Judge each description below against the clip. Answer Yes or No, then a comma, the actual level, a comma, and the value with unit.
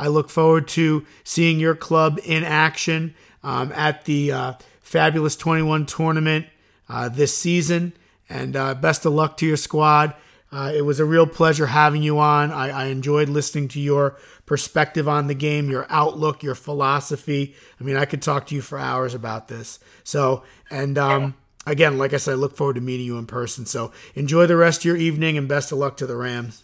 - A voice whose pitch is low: No, medium, 145 Hz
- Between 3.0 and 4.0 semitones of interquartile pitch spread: No, narrow, 2.4 semitones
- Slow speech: No, fast, 205 wpm